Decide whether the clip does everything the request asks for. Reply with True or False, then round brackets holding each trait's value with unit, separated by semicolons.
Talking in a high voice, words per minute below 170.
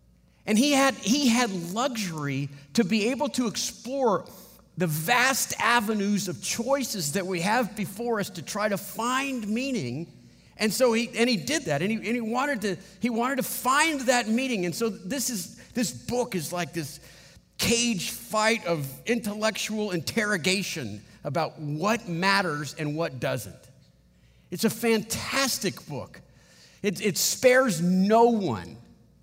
True (210 Hz; 150 wpm)